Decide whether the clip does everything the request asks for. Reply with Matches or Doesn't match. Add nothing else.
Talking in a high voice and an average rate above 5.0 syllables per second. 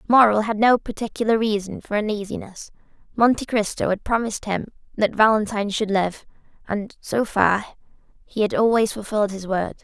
Matches